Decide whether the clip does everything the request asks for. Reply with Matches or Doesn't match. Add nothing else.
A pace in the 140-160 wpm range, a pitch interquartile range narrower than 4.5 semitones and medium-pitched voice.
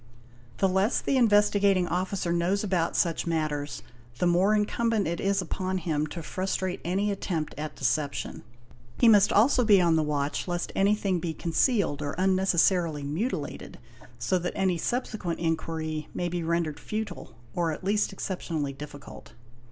Matches